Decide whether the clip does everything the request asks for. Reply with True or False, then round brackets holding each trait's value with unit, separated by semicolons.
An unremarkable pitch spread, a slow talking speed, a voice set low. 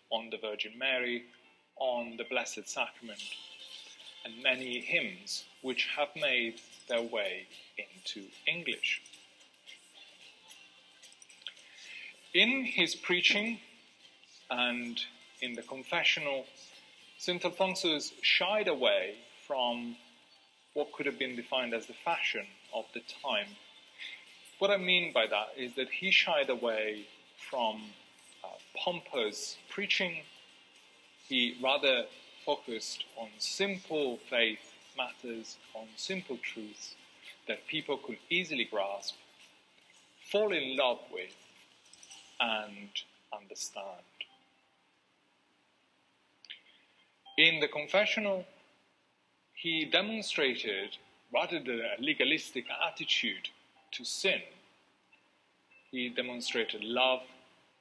False (7.3 semitones; 90 wpm; 130 Hz)